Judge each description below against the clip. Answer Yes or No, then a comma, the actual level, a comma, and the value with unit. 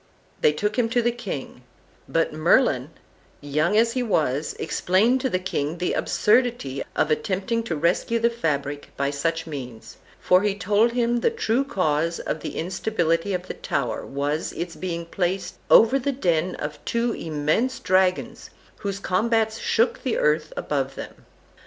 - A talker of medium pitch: Yes, medium, 180 Hz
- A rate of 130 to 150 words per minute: No, average, 160 wpm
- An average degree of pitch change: No, wide, 7.0 semitones